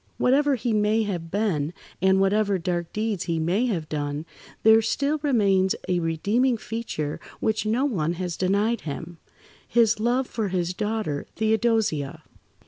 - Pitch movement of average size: Yes, average, 4.6 semitones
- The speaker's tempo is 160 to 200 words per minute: No, average, 140 wpm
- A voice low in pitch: No, high, 205 Hz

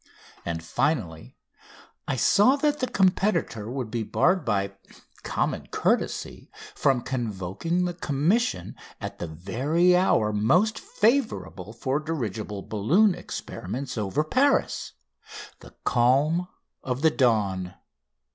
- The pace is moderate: No, slow, 110 wpm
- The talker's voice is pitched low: Yes, low, 130 Hz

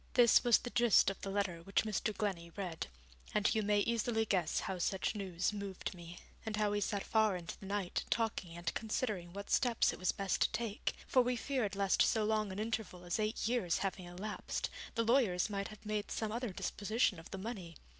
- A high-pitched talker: Yes, high, 205 Hz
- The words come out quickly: Yes, fast, 210 wpm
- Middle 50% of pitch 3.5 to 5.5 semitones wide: No, average, 3.0 semitones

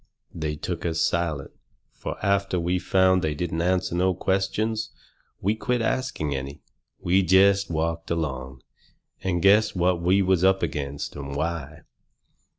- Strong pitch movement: No, average, 3.4 semitones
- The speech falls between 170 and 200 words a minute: No, average, 145 wpm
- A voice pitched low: Yes, very low, 90 Hz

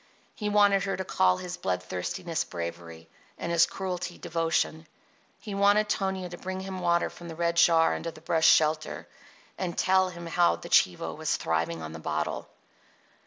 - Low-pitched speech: No, medium, 170 Hz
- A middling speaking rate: Yes, average, 170 wpm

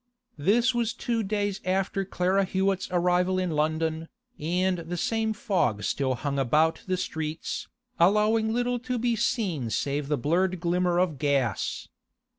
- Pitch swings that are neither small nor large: Yes, average, 4.9 semitones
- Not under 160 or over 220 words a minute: No, average, 145 wpm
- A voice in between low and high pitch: Yes, medium, 180 Hz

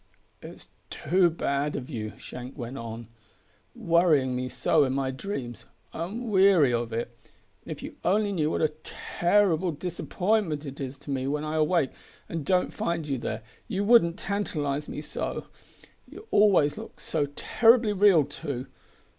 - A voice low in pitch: No, medium, 155 Hz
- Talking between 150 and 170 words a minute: Yes, average, 160 wpm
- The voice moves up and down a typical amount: No, wide, 5.7 semitones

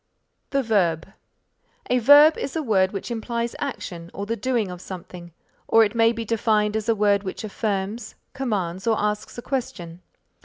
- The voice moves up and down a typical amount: Yes, average, 3.6 semitones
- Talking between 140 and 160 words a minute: No, average, 170 wpm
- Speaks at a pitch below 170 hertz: No, high, 215 Hz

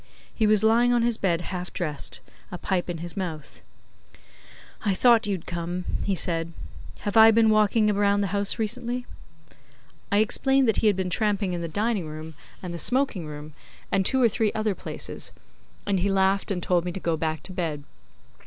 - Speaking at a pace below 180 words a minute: No, average, 190 wpm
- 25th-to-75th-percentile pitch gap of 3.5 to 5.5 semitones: Yes, average, 4.1 semitones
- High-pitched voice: Yes, high, 195 Hz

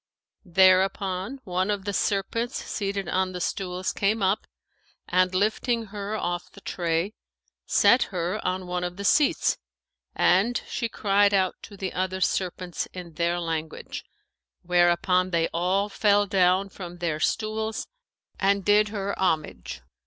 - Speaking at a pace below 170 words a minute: Yes, average, 145 wpm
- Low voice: No, high, 190 Hz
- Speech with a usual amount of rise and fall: No, narrow, 2.3 semitones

